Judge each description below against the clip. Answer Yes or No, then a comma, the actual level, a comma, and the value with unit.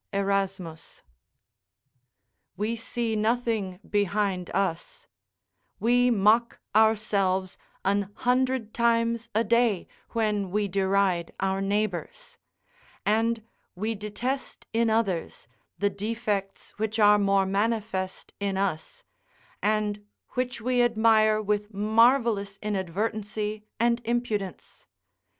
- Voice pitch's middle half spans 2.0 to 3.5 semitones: Yes, narrow, 2.6 semitones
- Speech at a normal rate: No, slow, 95 wpm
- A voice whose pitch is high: Yes, high, 210 Hz